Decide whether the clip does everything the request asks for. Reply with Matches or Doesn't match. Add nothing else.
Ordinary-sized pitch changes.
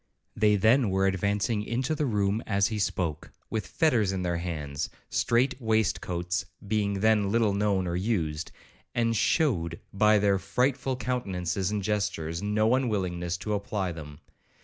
Matches